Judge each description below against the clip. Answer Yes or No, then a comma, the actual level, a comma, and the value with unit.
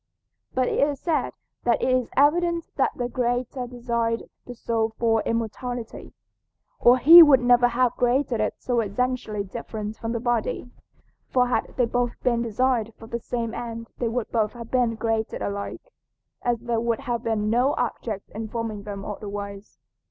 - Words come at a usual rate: Yes, average, 170 wpm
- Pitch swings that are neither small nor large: No, narrow, 1.8 semitones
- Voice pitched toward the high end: Yes, high, 235 Hz